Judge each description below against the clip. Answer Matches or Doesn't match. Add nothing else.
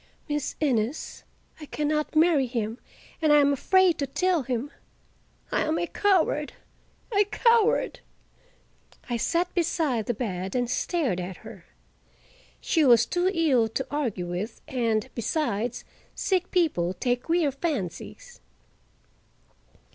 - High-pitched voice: Matches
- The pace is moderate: Doesn't match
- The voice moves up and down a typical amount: Doesn't match